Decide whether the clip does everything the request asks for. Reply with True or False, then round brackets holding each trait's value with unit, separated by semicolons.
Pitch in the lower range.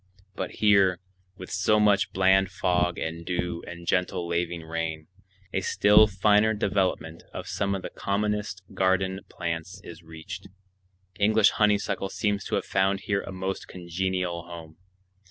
True (95 Hz)